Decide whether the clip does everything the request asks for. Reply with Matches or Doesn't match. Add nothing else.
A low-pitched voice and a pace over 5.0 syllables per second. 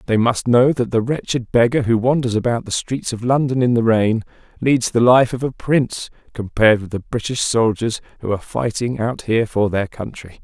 Matches